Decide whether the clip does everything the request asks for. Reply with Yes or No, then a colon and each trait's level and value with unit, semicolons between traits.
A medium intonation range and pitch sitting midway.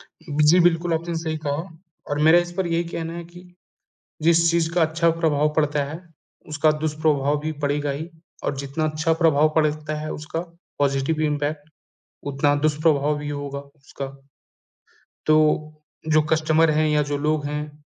No: narrow, 1.7 semitones; medium, 155 Hz